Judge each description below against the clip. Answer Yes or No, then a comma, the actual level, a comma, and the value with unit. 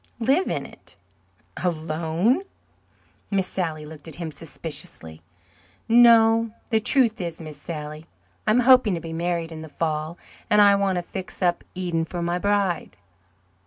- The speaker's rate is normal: Yes, average, 155 wpm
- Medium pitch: Yes, medium, 175 Hz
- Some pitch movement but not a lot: Yes, average, 4.5 semitones